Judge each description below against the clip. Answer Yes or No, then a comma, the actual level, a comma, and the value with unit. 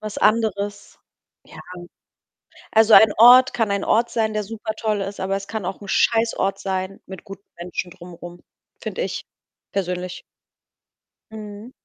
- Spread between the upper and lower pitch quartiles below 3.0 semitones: Yes, narrow, 2.5 semitones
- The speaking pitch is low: No, high, 205 Hz